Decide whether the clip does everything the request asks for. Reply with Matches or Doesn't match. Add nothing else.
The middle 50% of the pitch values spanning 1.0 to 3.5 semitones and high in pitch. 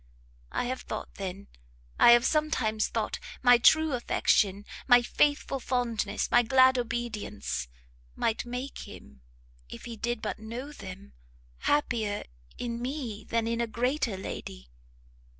Matches